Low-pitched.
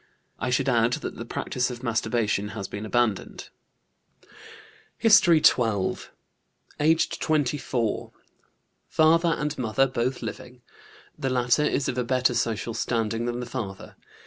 Yes: low, 125 Hz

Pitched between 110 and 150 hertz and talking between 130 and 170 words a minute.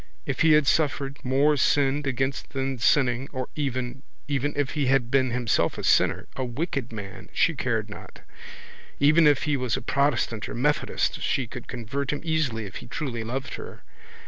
No: low, 135 Hz; average, 180 wpm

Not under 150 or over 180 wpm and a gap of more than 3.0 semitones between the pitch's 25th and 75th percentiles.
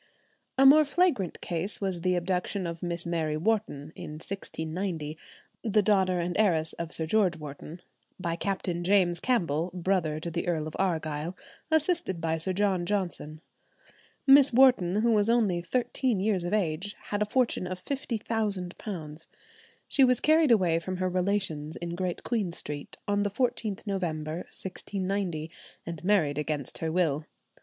Yes: average, 155 wpm; average, 4.0 semitones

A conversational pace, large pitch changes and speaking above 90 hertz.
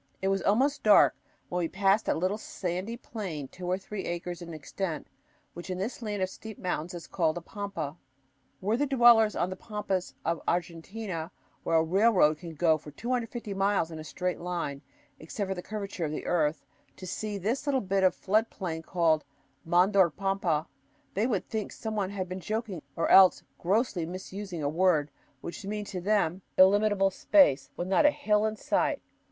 No: average, 190 wpm; average, 3.7 semitones; high, 190 Hz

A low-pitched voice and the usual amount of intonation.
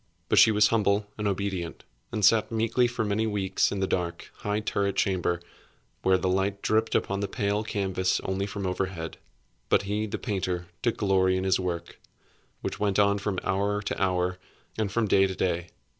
No: low, 100 Hz; narrow, 1.9 semitones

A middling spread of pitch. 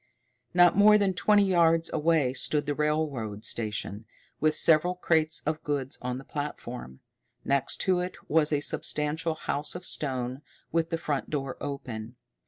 Yes: average, 3.7 semitones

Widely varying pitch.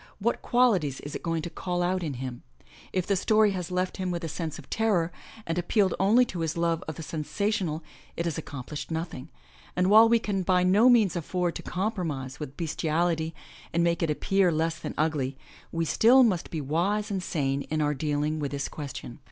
No: average, 3.7 semitones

